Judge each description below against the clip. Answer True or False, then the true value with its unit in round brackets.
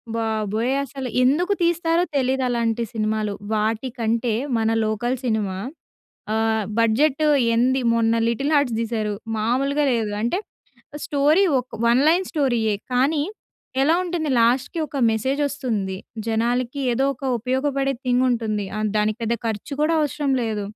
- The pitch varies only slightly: False (3.9 semitones)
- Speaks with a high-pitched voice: True (240 Hz)